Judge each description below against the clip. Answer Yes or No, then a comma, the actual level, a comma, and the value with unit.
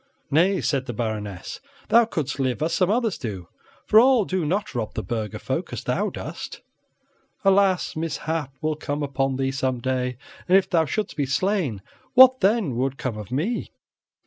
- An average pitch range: No, wide, 7.1 semitones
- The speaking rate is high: No, average, 175 wpm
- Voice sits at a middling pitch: Yes, medium, 145 Hz